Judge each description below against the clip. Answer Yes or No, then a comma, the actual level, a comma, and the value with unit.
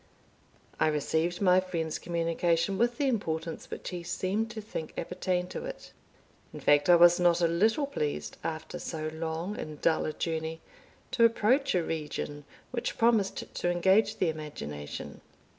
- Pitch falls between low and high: Yes, medium, 175 Hz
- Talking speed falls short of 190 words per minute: Yes, average, 160 wpm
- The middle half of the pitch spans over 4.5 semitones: No, average, 4.2 semitones